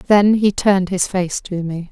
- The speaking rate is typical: No, fast, 220 wpm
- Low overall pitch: No, high, 190 Hz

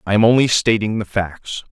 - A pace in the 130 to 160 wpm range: No, fast, 205 wpm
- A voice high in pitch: No, low, 105 Hz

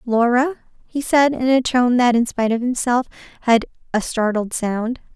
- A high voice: Yes, high, 240 Hz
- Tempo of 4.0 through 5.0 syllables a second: Yes, 4.7 syllables/s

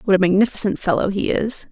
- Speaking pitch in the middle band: No, high, 195 Hz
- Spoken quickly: Yes, fast, 210 wpm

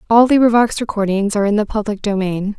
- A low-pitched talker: No, high, 210 Hz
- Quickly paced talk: No, average, 185 wpm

